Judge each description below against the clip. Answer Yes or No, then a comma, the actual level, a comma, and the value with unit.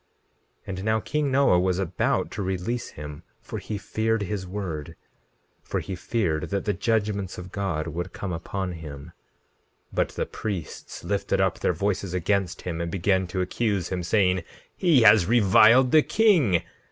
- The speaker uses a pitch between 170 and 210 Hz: No, very low, 95 Hz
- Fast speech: No, average, 170 wpm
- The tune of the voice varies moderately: Yes, average, 3.6 semitones